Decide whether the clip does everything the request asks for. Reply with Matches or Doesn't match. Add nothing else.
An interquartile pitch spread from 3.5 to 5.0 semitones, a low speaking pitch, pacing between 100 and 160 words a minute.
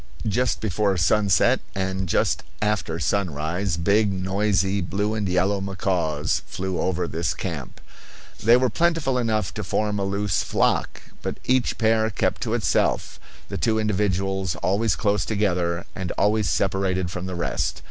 Doesn't match